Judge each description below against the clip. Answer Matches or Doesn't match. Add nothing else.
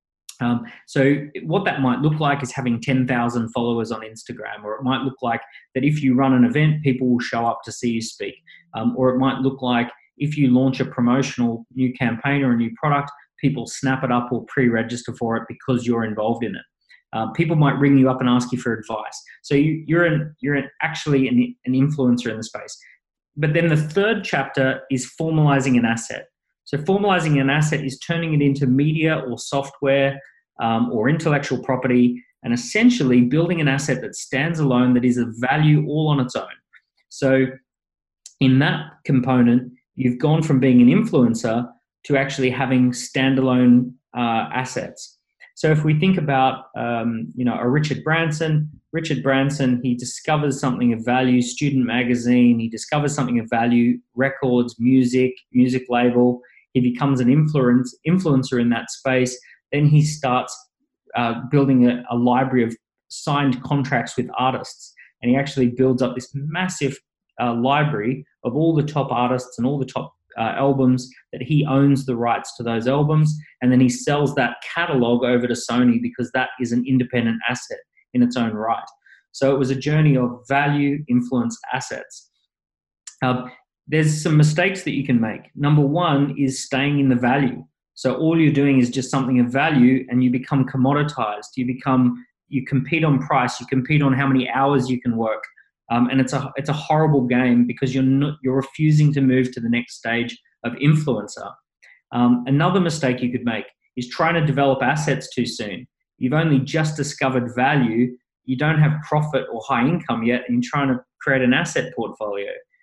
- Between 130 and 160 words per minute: Doesn't match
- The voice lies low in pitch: Matches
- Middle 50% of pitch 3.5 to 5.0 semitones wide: Doesn't match